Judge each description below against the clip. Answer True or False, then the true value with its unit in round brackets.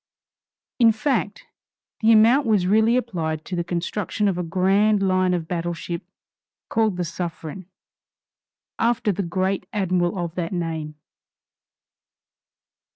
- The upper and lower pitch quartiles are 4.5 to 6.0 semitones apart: False (3.8 semitones)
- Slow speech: True (125 wpm)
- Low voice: False (185 Hz)